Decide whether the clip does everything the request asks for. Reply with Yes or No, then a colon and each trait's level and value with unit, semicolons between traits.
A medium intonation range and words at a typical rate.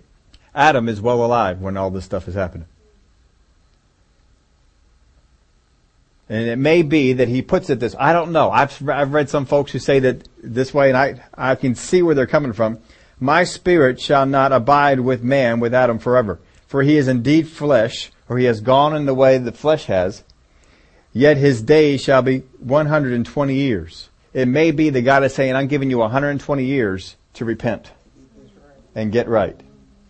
No: wide, 6.6 semitones; average, 180 wpm